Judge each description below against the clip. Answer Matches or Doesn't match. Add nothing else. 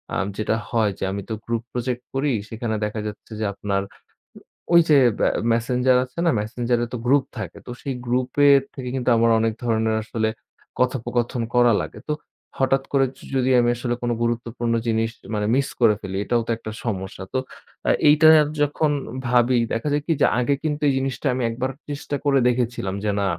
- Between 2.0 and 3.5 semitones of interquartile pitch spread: Matches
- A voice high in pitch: Doesn't match